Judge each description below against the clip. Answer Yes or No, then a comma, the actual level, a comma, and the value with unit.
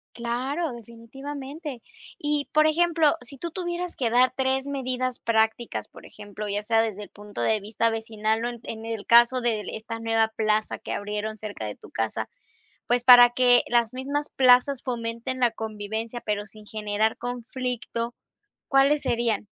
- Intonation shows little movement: No, average, 3.1 semitones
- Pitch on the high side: Yes, high, 235 Hz